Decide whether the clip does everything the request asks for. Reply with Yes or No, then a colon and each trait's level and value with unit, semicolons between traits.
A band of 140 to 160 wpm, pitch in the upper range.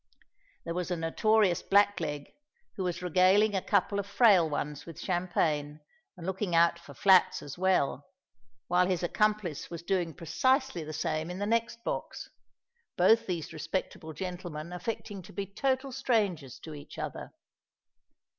No: average, 150 wpm; medium, 180 Hz